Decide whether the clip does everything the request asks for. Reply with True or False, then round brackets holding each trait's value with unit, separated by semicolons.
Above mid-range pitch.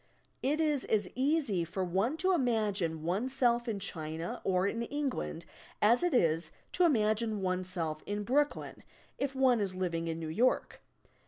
True (210 Hz)